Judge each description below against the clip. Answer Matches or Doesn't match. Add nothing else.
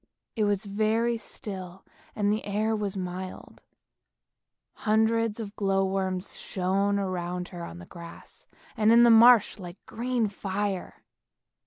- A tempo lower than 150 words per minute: Matches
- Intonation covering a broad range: Doesn't match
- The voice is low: Doesn't match